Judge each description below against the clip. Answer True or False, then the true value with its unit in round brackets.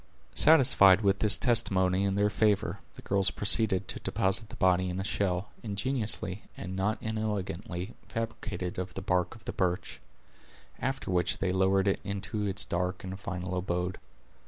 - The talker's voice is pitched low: True (95 Hz)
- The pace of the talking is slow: False (160 wpm)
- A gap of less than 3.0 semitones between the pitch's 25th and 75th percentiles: True (2.4 semitones)